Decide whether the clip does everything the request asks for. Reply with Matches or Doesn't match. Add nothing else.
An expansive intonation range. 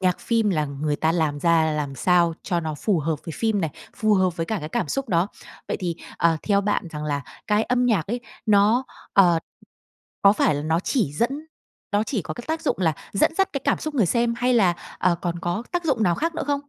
Matches